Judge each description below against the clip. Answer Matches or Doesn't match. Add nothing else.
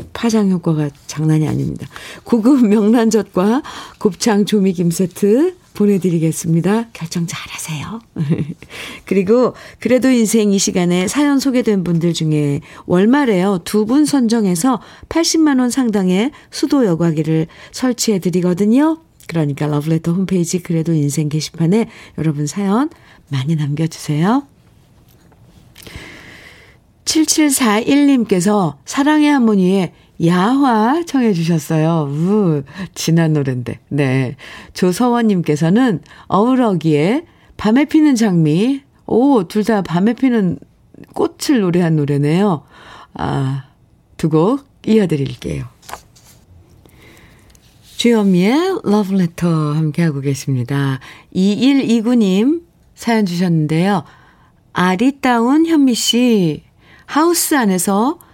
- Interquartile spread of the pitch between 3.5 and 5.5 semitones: Doesn't match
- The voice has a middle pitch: Doesn't match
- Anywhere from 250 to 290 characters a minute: Doesn't match